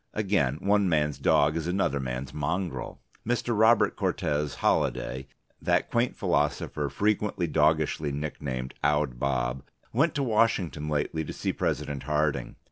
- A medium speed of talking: No, slow, 130 wpm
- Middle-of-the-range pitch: No, very low, 75 Hz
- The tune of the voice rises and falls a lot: Yes, wide, 6.1 semitones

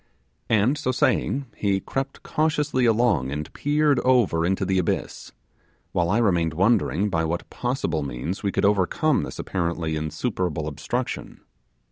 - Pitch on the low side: Yes, low, 100 Hz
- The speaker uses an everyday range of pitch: No, wide, 7.2 semitones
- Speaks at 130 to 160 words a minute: Yes, average, 140 wpm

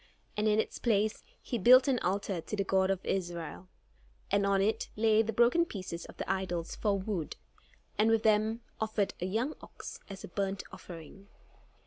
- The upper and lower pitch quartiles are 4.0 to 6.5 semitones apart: No, average, 2.7 semitones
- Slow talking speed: No, average, 180 wpm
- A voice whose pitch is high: Yes, high, 200 Hz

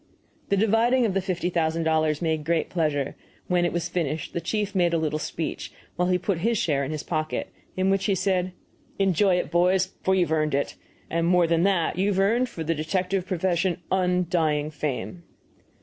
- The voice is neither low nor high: Yes, medium, 175 Hz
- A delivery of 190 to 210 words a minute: Yes, average, 195 wpm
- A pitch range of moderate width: Yes, average, 3.0 semitones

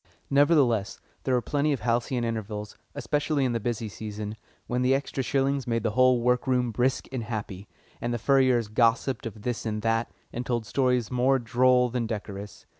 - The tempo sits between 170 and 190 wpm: Yes, average, 185 wpm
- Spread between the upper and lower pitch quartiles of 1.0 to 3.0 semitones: Yes, narrow, 2.5 semitones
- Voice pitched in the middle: No, low, 120 Hz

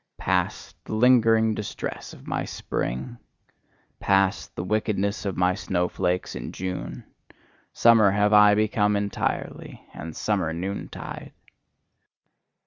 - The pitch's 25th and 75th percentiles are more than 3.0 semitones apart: No, average, 2.7 semitones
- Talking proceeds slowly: Yes, slow, 110 wpm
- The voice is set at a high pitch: No, low, 100 Hz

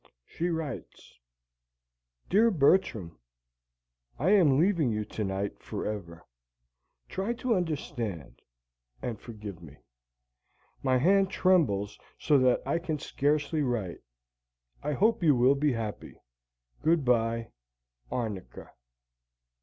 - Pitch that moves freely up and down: Yes, wide, 7.8 semitones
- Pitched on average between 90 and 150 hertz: Yes, low, 135 Hz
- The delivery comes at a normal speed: No, slow, 105 wpm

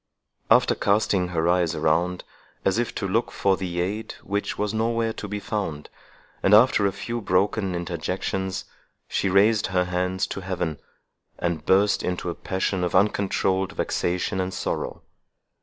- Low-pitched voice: Yes, very low, 95 Hz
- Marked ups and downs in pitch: No, narrow, 2.4 semitones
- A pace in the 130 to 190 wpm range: Yes, average, 155 wpm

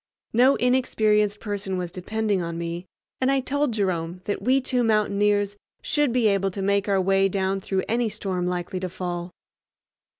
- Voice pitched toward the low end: No, high, 200 Hz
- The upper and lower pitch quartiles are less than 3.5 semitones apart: Yes, average, 3.1 semitones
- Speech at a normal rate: Yes, average, 170 wpm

